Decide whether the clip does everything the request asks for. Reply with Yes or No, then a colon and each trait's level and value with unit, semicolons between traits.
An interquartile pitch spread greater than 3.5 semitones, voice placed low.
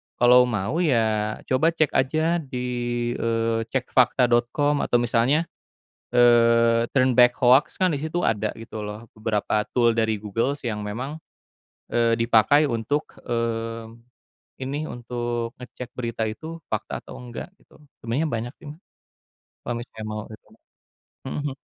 No: narrow, 2.5 semitones; low, 120 Hz